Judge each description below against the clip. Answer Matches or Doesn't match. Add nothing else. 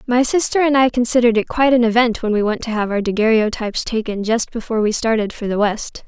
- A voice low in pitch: Doesn't match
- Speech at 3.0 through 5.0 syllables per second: Doesn't match